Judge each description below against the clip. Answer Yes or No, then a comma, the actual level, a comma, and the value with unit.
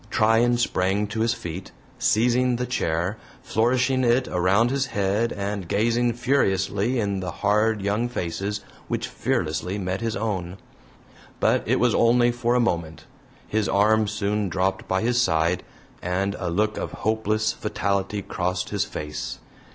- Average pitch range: Yes, average, 3.7 semitones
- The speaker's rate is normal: Yes, average, 150 wpm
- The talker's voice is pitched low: Yes, low, 105 Hz